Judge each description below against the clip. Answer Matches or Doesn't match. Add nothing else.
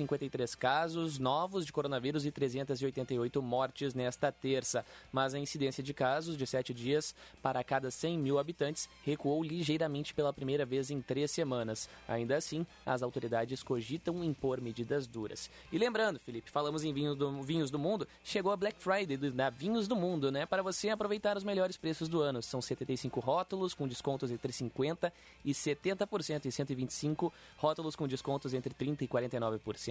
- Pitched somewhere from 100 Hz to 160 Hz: Matches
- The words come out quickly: Doesn't match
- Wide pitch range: Doesn't match